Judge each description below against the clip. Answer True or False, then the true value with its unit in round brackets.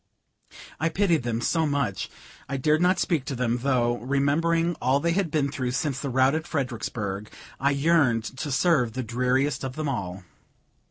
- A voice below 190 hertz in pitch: True (140 Hz)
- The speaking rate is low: False (175 wpm)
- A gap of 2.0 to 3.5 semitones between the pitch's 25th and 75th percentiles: False (4.2 semitones)